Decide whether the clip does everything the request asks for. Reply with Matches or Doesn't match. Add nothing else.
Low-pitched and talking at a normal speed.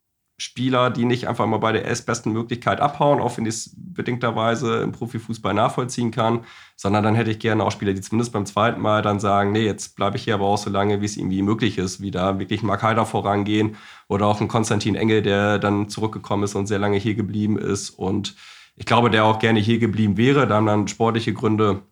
Doesn't match